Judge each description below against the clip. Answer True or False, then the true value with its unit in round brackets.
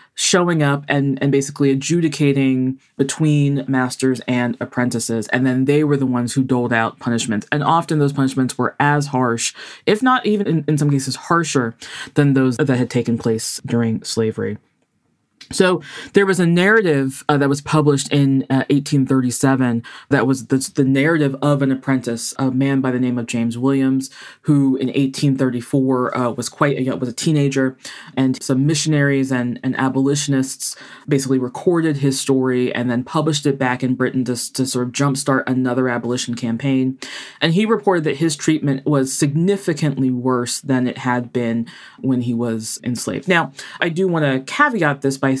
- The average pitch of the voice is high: False (135 Hz)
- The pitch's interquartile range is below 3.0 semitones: True (2.4 semitones)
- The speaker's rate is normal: True (175 wpm)